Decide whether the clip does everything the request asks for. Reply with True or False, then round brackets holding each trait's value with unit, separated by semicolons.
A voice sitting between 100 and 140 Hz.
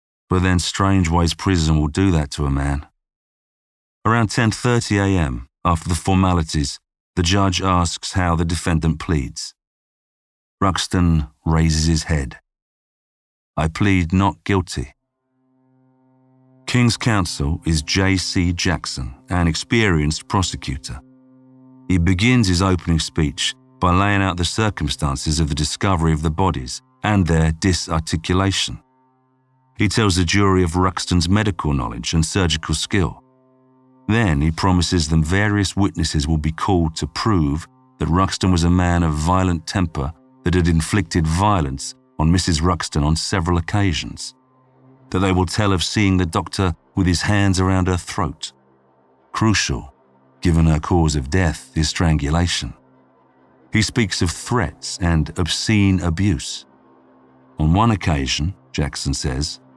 False (90 Hz)